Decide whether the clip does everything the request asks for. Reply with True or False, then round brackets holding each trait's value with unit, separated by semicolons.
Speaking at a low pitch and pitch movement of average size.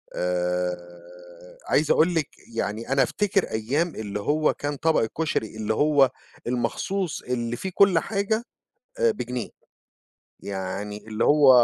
False (125 Hz; 7.7 semitones)